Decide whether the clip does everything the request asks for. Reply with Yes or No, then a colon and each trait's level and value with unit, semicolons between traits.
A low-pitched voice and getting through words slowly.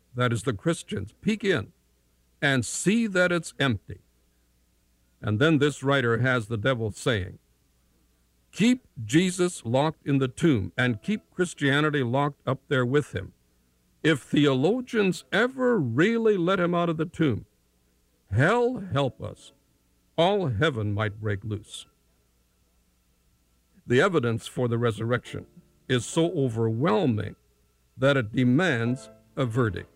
Yes: low, 125 Hz; slow, 130 wpm